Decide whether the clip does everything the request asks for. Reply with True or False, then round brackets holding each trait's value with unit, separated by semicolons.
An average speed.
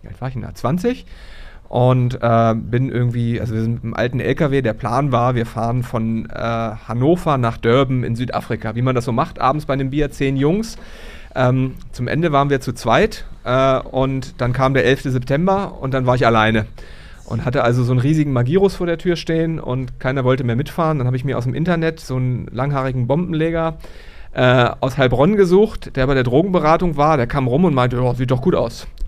False (215 wpm)